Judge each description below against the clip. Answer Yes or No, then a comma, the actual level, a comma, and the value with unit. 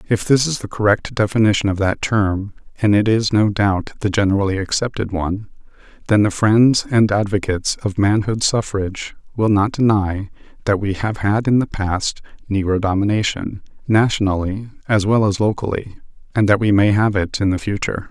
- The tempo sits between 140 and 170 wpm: Yes, average, 165 wpm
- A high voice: No, low, 105 Hz